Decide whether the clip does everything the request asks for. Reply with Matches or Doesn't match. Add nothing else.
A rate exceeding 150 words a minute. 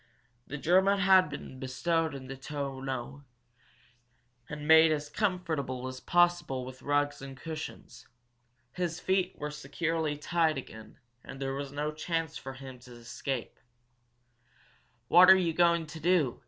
Doesn't match